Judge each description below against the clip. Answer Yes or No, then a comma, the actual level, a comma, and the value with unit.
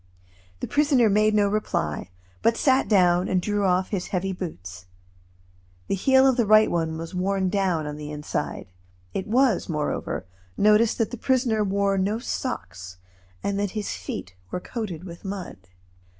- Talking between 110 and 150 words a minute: No, average, 165 wpm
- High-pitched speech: Yes, high, 195 Hz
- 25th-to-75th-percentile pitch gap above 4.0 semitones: No, average, 3.7 semitones